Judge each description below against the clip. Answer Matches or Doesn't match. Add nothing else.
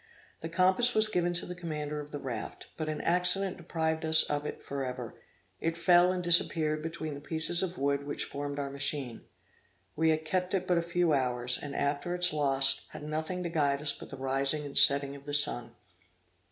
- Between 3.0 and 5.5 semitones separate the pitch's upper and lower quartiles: Matches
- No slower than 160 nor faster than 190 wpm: Doesn't match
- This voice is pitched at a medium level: Matches